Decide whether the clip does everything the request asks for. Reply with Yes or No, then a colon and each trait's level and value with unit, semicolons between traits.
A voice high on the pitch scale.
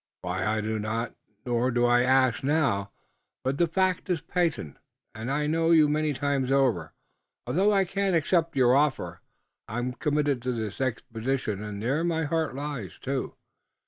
No: low, 135 Hz